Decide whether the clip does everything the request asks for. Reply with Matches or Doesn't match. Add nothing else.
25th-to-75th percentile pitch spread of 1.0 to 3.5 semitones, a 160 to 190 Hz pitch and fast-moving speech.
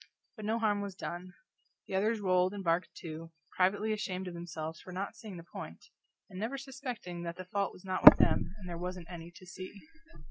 Matches